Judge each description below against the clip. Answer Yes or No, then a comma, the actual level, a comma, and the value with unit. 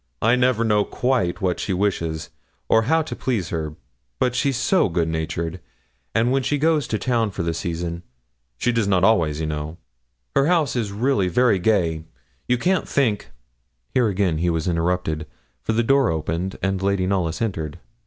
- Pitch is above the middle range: No, very low, 95 Hz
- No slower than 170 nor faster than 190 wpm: Yes, average, 185 wpm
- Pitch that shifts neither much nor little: No, wide, 6.6 semitones